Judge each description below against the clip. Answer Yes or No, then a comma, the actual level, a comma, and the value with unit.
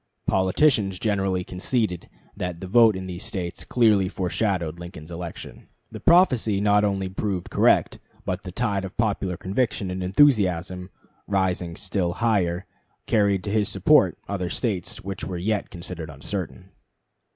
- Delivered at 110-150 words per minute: Yes, average, 140 wpm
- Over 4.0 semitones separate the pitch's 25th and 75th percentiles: No, narrow, 2.5 semitones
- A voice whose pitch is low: Yes, very low, 95 Hz